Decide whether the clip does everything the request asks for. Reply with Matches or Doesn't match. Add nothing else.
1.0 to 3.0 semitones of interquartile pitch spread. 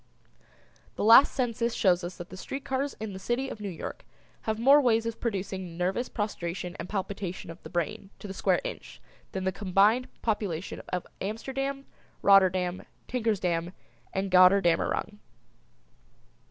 Doesn't match